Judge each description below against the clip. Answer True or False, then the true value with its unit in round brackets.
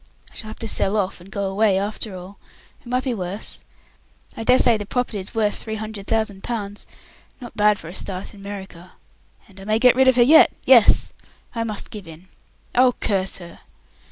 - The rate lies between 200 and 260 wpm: True (205 wpm)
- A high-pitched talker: True (210 Hz)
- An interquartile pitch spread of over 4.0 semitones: False (2.9 semitones)